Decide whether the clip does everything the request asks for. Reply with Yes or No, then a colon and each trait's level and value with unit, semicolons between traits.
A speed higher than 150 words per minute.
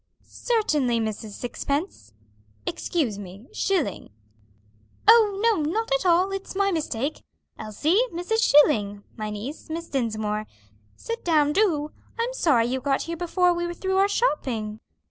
No: average, 140 wpm